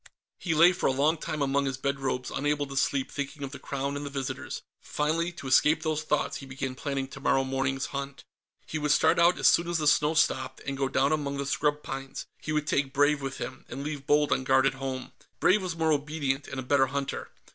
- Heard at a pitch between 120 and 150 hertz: Yes, medium, 140 Hz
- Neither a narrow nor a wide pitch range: No, narrow, 2.0 semitones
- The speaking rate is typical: No, fast, 235 wpm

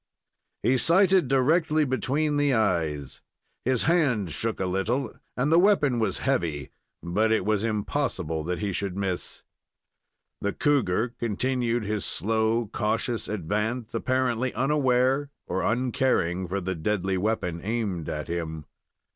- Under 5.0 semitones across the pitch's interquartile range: No, wide, 5.6 semitones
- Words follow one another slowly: Yes, slow, 130 wpm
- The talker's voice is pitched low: Yes, low, 110 Hz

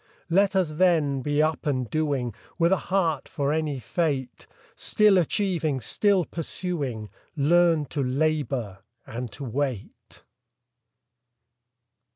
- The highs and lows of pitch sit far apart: No, average, 4.6 semitones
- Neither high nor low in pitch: Yes, medium, 150 Hz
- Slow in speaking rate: Yes, slow, 115 wpm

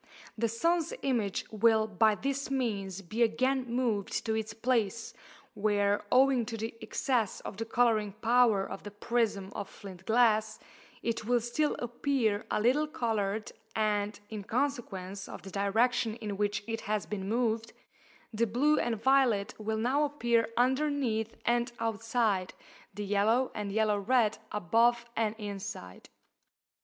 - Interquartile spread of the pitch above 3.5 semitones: No, average, 2.8 semitones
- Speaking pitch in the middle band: No, high, 225 Hz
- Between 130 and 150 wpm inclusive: Yes, average, 145 wpm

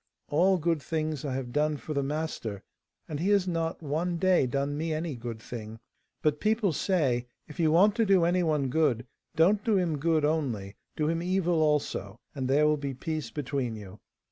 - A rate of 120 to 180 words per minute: No, average, 195 wpm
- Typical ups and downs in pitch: Yes, average, 3.8 semitones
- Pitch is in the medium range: Yes, medium, 155 Hz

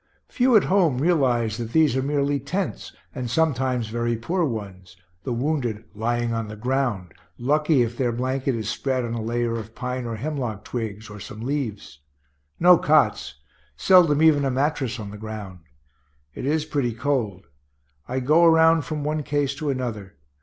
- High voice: No, low, 125 Hz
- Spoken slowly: No, average, 170 wpm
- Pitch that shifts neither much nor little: Yes, average, 4.6 semitones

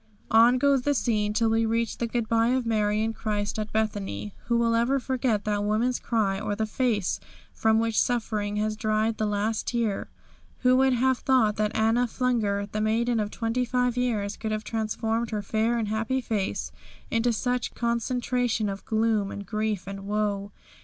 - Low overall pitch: No, high, 220 Hz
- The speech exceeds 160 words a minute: Yes, average, 180 wpm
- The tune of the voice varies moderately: No, narrow, 2.1 semitones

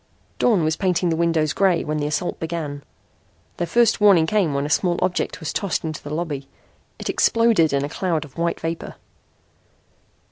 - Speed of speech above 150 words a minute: Yes, average, 180 wpm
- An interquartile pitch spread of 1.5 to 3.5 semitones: Yes, average, 3.2 semitones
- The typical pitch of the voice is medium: Yes, medium, 165 Hz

